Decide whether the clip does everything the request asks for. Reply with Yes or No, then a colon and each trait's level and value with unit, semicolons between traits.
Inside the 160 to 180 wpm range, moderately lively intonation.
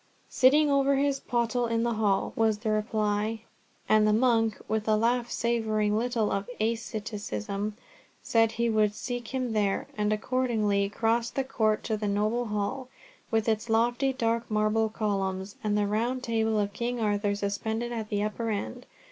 No: average, 165 wpm; narrow, 2.1 semitones